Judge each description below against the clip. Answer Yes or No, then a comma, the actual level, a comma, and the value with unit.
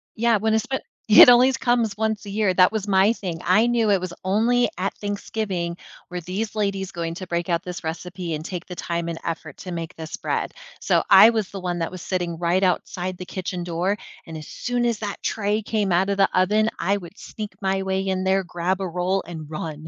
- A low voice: No, high, 190 Hz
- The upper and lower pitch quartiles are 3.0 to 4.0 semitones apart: Yes, average, 3.4 semitones